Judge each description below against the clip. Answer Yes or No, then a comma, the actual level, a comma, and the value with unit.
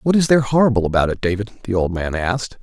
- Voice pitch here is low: Yes, low, 110 Hz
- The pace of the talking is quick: Yes, fast, 250 wpm